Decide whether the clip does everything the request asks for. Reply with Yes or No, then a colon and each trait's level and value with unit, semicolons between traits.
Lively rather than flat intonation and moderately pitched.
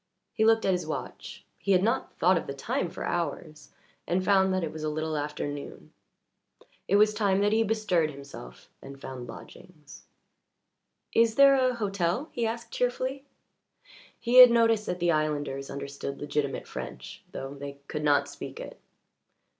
Yes: wide, 7.2 semitones; medium, 180 Hz